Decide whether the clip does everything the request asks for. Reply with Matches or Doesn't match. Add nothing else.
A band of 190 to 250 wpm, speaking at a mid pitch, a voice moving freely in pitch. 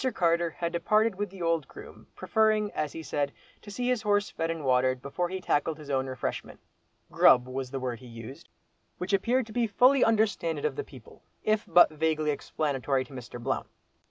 Matches